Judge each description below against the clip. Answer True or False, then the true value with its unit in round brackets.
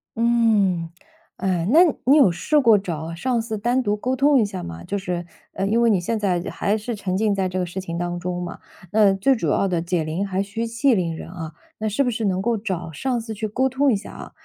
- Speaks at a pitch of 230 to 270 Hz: False (200 Hz)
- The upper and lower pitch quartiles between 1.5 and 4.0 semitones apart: False (4.5 semitones)